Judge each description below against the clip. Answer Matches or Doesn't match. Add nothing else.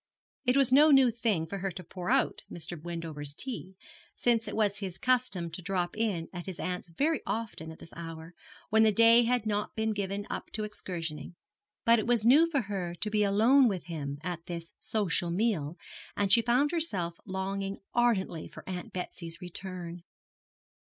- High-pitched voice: Matches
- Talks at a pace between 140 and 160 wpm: Doesn't match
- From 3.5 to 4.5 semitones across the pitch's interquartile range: Doesn't match